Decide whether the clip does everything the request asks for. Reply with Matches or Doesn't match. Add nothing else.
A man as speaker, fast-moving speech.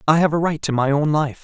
Matches